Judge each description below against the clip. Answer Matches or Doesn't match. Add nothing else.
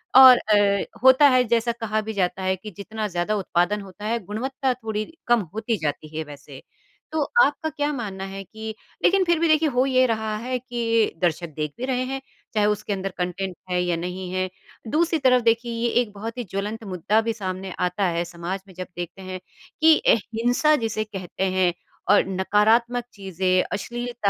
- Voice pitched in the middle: Doesn't match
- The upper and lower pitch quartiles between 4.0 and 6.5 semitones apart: Matches